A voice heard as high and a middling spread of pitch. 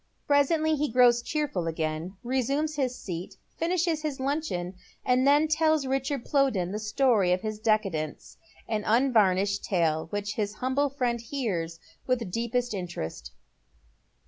No: high, 235 Hz; wide, 6.5 semitones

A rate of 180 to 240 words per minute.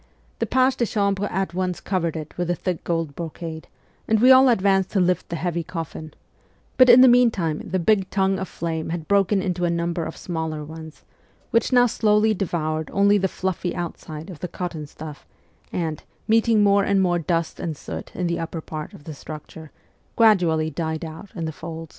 Yes: average, 200 wpm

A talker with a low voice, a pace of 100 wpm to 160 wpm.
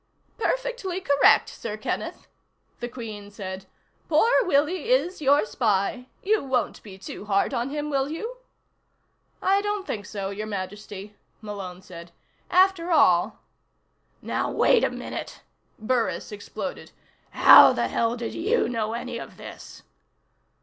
No: high, 240 Hz; slow, 135 wpm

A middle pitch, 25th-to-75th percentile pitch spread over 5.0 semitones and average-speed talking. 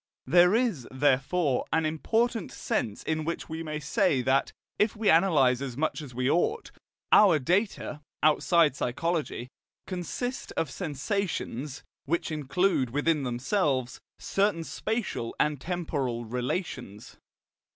No: medium, 155 Hz; wide, 5.4 semitones; slow, 120 wpm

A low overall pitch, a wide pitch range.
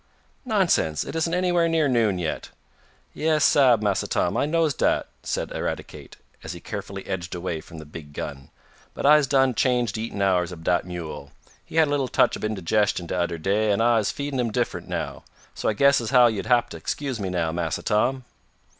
Yes: low, 110 Hz; wide, 7.8 semitones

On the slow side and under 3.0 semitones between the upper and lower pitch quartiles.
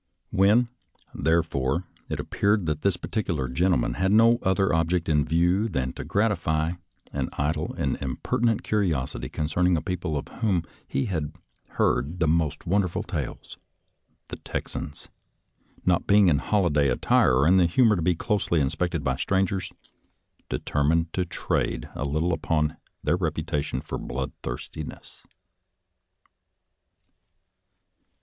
No: slow, 130 wpm; average, 4.2 semitones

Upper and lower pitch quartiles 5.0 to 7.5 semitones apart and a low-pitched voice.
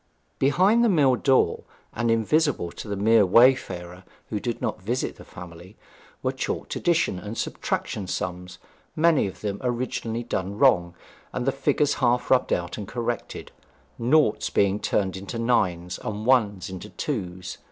Yes: wide, 5.5 semitones; low, 110 Hz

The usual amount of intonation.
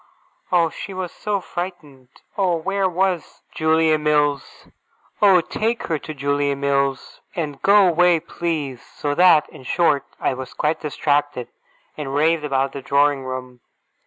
Yes: average, 3.9 semitones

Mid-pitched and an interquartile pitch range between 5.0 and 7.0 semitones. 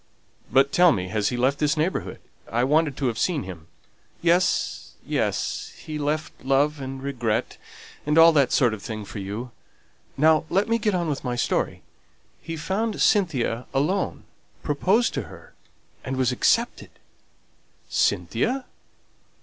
Yes: medium, 145 Hz; average, 5.3 semitones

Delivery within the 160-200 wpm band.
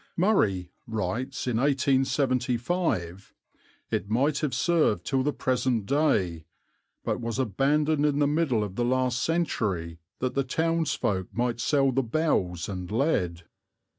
No: slow, 135 wpm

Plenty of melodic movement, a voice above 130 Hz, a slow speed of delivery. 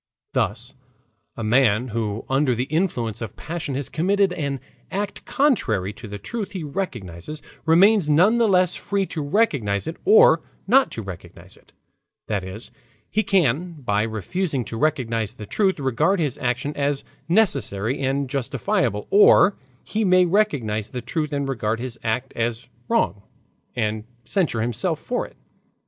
No: wide, 8.3 semitones; medium, 140 Hz; average, 155 wpm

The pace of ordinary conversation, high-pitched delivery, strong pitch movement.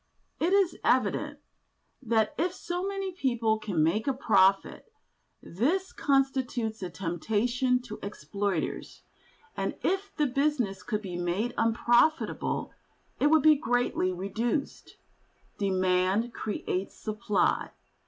No: slow, 115 wpm; high, 235 Hz; wide, 6.3 semitones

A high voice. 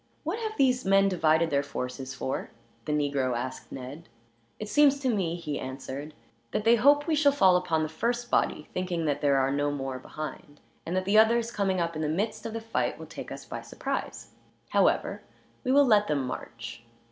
No: medium, 170 Hz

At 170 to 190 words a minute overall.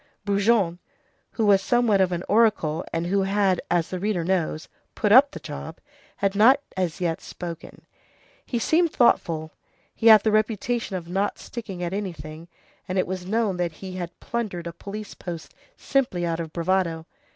Yes: average, 175 wpm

